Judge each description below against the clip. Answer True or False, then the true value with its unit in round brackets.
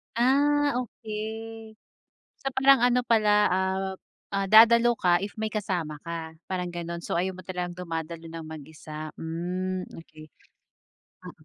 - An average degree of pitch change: True (4.8 semitones)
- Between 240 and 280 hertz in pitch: False (185 Hz)